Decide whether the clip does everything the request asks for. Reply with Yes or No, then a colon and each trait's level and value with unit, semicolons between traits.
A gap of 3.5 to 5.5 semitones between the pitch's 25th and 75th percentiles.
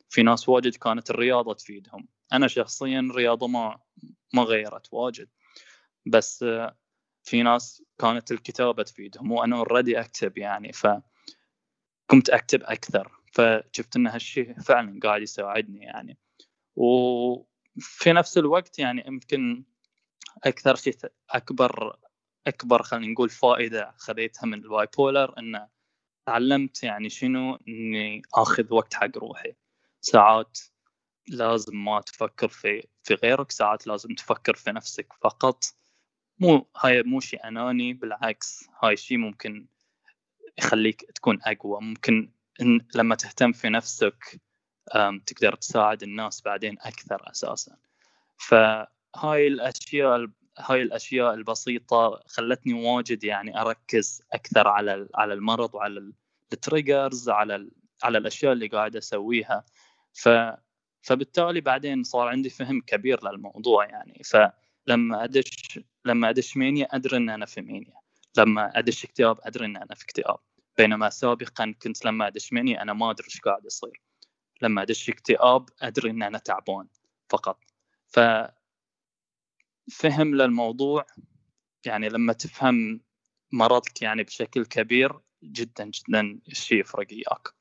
No: average, 3.0 semitones